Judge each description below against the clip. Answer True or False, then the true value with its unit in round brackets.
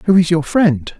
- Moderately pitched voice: True (170 Hz)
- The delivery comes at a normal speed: False (240 wpm)